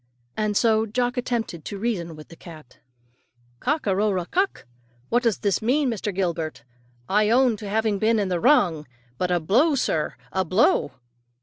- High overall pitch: Yes, high, 210 Hz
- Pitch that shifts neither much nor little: Yes, average, 5.0 semitones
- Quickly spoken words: No, average, 180 wpm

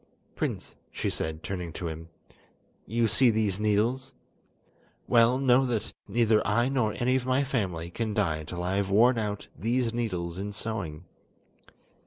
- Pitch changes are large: No, average, 4.6 semitones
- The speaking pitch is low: Yes, low, 110 Hz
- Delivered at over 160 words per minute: No, average, 155 wpm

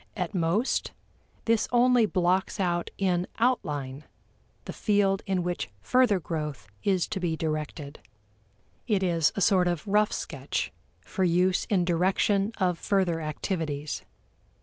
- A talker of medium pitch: Yes, medium, 180 Hz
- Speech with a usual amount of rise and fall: Yes, average, 3.4 semitones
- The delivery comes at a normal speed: No, slow, 130 wpm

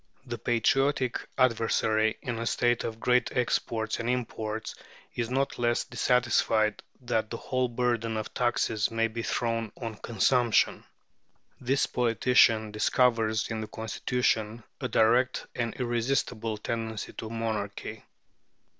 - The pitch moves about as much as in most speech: No, narrow, 1.9 semitones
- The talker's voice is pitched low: Yes, low, 115 Hz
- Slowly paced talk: Yes, slow, 125 wpm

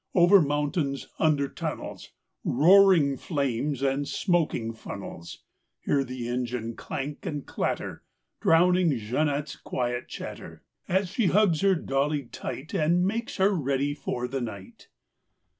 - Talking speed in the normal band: No, slow, 125 wpm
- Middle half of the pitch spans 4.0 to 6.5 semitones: Yes, average, 5.1 semitones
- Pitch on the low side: No, medium, 145 Hz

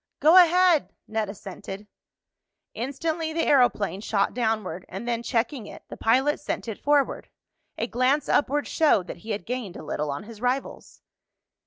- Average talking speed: Yes, average, 160 wpm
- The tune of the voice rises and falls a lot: Yes, wide, 5.9 semitones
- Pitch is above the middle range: Yes, high, 240 Hz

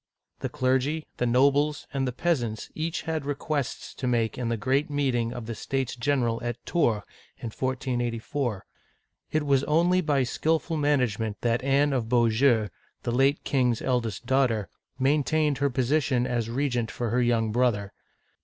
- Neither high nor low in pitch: No, low, 130 Hz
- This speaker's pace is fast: No, average, 165 wpm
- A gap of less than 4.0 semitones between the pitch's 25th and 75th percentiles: Yes, average, 3.3 semitones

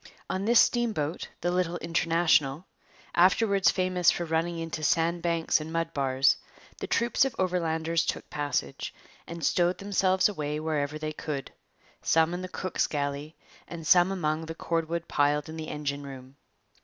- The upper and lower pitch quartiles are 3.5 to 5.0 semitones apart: No, average, 2.7 semitones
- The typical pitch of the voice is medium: Yes, medium, 165 Hz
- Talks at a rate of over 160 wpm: No, average, 155 wpm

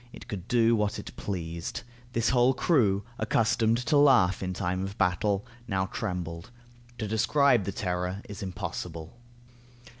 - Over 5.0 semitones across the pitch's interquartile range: No, average, 4.0 semitones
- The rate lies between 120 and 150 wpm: Yes, average, 145 wpm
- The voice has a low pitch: Yes, low, 100 Hz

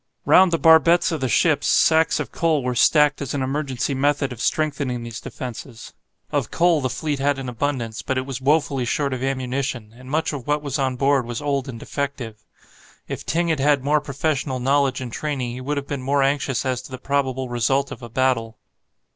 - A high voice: No, low, 135 Hz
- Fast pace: Yes, fast, 210 wpm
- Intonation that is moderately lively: No, narrow, 2.3 semitones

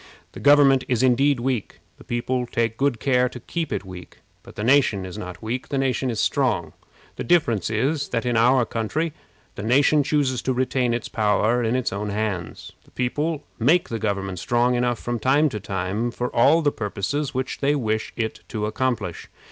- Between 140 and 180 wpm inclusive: No, average, 195 wpm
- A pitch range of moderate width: Yes, average, 3.7 semitones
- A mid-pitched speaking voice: No, low, 120 Hz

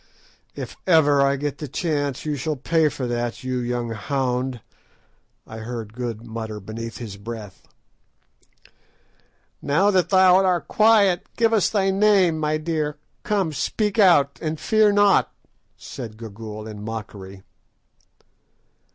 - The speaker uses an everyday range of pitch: No, wide, 7.7 semitones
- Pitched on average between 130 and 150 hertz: Yes, medium, 140 Hz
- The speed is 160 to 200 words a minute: No, slow, 135 wpm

